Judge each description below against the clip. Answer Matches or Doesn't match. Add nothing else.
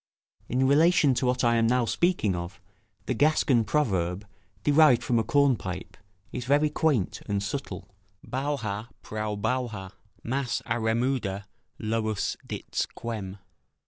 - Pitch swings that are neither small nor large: Matches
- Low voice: Matches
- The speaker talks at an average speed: Doesn't match